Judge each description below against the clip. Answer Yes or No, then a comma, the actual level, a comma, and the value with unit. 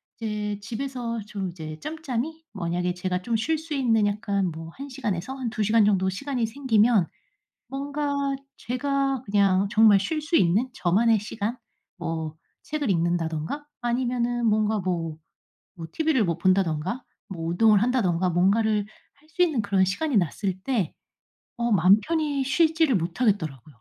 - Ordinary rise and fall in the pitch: No, wide, 6.0 semitones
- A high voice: Yes, high, 215 Hz